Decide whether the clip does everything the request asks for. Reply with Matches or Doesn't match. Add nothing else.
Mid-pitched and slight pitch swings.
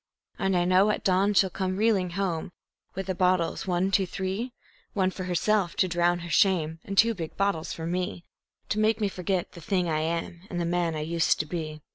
Matches